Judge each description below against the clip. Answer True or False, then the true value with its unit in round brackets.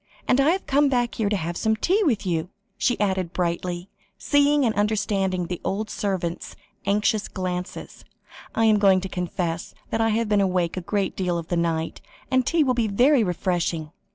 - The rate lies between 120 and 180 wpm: False (190 wpm)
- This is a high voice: True (200 Hz)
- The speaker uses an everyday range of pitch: True (4.1 semitones)